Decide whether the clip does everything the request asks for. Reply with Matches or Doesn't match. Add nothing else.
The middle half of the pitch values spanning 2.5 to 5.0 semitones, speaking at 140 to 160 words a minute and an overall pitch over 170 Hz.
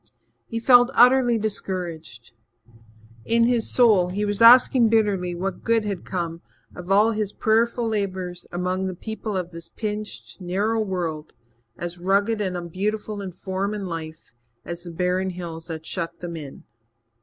Matches